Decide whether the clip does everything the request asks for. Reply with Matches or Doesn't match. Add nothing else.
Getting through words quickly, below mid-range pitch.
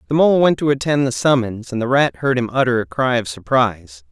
Matches